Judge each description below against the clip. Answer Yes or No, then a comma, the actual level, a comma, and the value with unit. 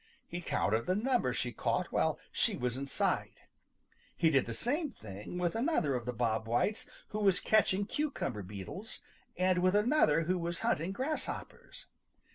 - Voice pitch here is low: No, medium, 175 Hz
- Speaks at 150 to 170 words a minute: Yes, average, 165 wpm